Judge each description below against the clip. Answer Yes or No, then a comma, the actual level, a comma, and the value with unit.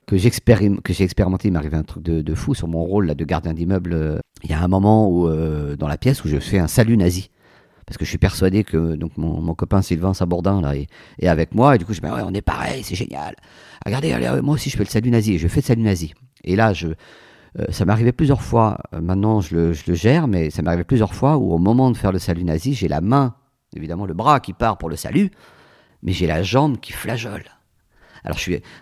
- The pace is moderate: No, fast, 260 wpm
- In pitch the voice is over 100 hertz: No, very low, 95 Hz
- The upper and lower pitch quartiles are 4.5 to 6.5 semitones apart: Yes, average, 5.2 semitones